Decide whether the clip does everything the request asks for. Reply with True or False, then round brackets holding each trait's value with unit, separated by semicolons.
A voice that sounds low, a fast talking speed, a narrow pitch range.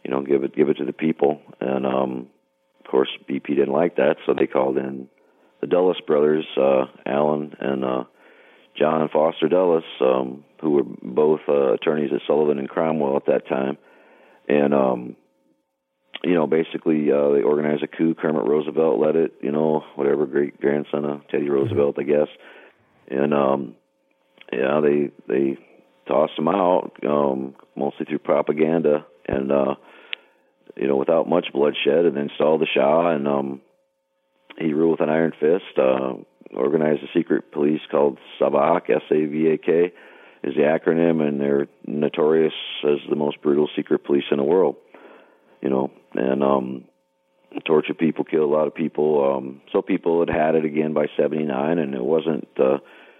False (70 Hz; 170 wpm; 2.3 semitones)